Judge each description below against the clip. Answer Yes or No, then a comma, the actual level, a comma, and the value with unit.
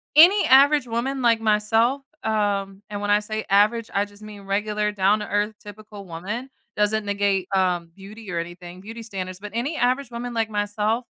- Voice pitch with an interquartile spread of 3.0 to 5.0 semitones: No, narrow, 2.5 semitones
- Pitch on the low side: No, high, 210 Hz